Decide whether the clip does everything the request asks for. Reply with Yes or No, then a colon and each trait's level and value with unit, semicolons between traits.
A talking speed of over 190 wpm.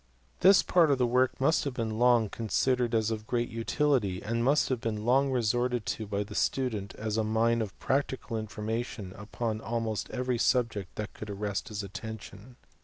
No: average, 185 wpm